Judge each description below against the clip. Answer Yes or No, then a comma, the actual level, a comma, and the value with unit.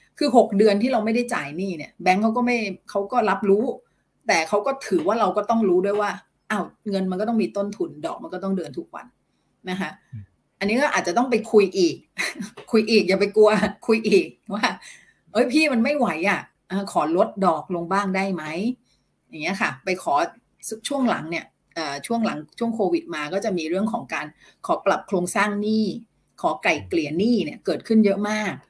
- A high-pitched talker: Yes, high, 205 Hz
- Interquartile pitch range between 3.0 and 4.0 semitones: Yes, average, 3.4 semitones